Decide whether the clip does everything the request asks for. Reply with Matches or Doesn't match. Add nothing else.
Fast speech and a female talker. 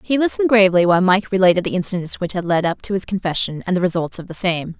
Matches